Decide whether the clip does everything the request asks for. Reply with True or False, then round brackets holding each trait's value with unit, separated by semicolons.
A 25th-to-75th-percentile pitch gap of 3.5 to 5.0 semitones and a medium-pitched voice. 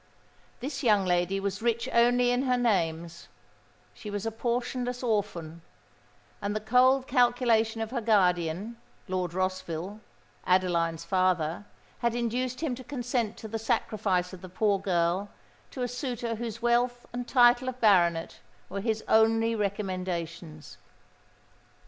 False (4.7 semitones; 220 Hz)